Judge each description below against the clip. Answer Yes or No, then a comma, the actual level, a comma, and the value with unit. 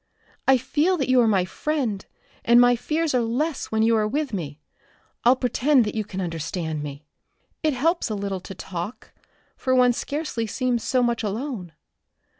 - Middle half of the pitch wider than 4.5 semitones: Yes, average, 5.1 semitones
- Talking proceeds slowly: No, average, 180 wpm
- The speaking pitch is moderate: No, high, 235 Hz